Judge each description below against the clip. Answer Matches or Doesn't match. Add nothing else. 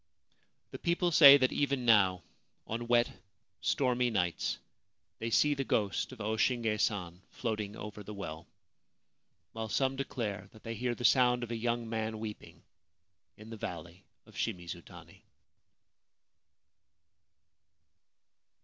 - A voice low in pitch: Matches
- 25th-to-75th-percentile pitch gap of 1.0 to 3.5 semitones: Matches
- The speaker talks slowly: Matches